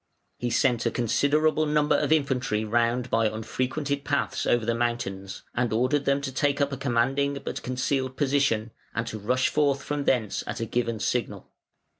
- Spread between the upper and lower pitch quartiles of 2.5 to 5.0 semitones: Yes, average, 3.4 semitones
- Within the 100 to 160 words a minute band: No, average, 175 wpm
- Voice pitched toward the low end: Yes, low, 125 Hz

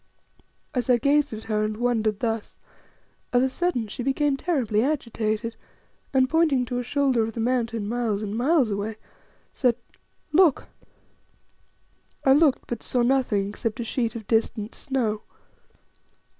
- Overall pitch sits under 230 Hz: No, high, 240 Hz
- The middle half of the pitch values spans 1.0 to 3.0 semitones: No, average, 3.4 semitones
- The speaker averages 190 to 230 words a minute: No, average, 145 wpm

